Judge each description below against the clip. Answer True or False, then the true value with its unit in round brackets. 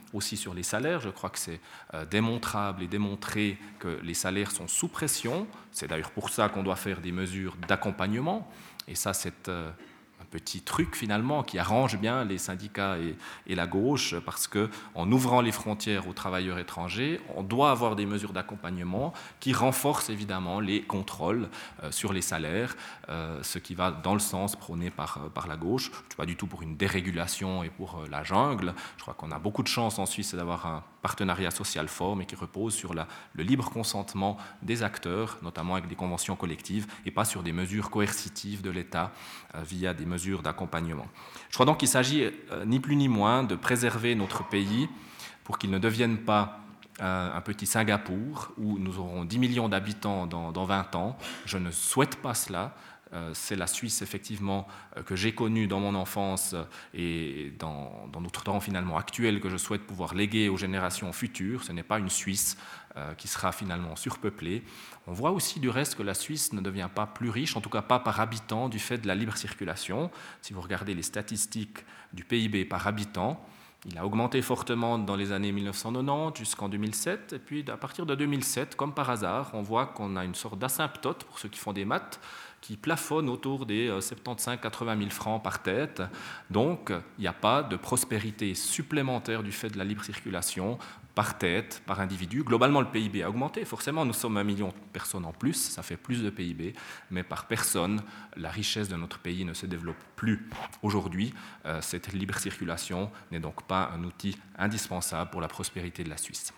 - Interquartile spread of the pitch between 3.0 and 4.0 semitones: True (3.4 semitones)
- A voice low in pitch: True (100 Hz)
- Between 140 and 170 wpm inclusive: False (195 wpm)